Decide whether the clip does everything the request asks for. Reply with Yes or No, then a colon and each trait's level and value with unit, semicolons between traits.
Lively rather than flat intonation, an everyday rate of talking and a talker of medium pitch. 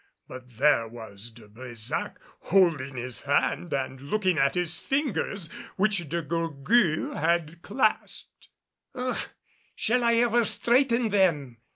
No: wide, 8.4 semitones; slow, 125 wpm; medium, 165 Hz